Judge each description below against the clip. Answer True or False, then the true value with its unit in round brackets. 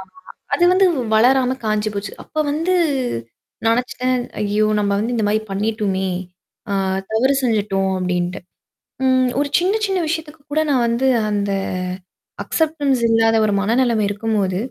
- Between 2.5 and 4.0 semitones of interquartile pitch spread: False (4.4 semitones)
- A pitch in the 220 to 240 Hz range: True (225 Hz)